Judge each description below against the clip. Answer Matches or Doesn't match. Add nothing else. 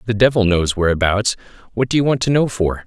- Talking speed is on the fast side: Matches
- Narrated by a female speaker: Doesn't match